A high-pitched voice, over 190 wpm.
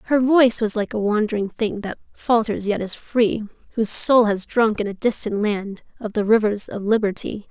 Yes: high, 215 Hz; average, 200 wpm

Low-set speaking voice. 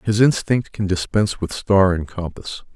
Yes: low, 100 Hz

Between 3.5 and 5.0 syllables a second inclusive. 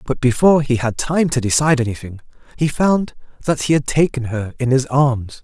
No: 5.4 syllables/s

